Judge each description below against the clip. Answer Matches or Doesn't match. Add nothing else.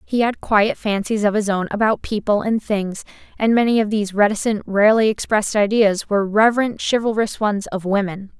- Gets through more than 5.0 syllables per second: Matches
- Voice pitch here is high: Matches